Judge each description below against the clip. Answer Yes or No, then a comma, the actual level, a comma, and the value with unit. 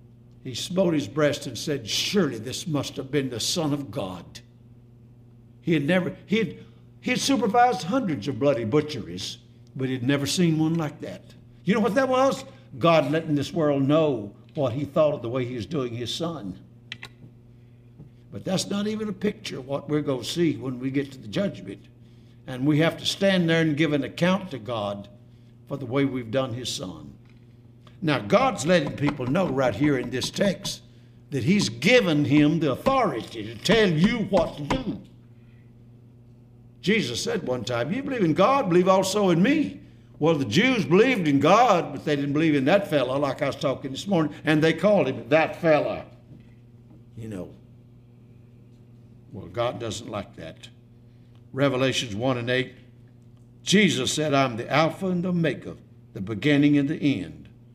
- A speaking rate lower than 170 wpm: No, average, 180 wpm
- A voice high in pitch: No, low, 135 Hz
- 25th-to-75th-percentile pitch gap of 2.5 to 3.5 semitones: No, average, 5.1 semitones